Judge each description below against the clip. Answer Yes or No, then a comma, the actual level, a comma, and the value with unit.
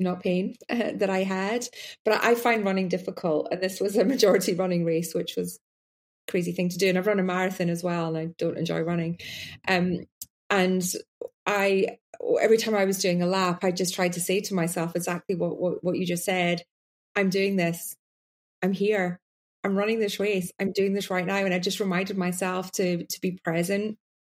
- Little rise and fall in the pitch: Yes, narrow, 2.3 semitones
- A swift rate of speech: Yes, fast, 210 wpm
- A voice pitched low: No, medium, 185 Hz